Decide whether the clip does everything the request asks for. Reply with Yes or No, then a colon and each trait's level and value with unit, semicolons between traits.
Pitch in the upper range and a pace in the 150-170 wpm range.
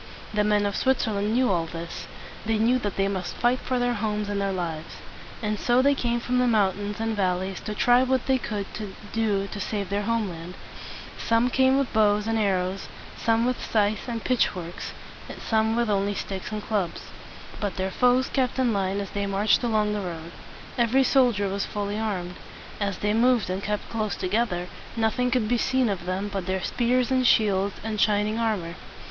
No: high, 210 Hz; average, 195 wpm